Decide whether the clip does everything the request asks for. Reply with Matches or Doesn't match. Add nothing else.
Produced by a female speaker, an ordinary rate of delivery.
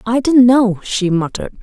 Matches